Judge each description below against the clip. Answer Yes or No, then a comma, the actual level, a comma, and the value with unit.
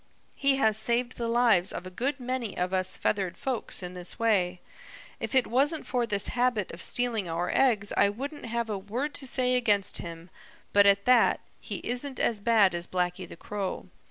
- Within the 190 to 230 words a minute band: Yes, average, 195 wpm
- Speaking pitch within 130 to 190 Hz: No, high, 220 Hz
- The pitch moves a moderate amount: Yes, average, 4.9 semitones